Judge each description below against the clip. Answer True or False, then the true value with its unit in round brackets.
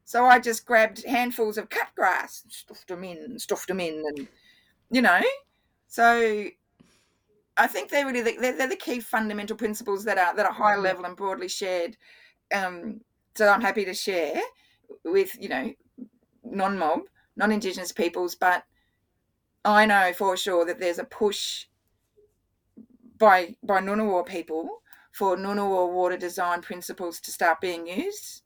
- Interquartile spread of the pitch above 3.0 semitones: True (4.8 semitones)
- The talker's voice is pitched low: False (205 Hz)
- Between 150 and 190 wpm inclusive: True (155 wpm)